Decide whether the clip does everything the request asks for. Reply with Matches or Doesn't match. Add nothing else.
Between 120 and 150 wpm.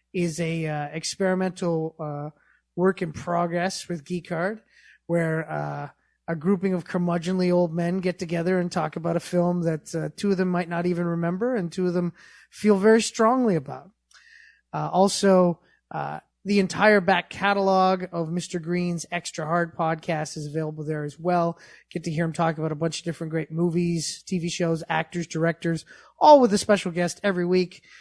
Doesn't match